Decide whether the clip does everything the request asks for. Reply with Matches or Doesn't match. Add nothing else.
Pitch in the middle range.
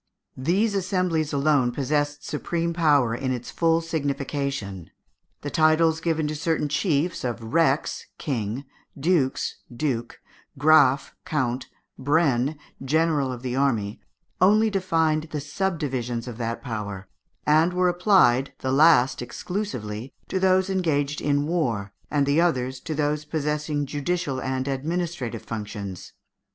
Matches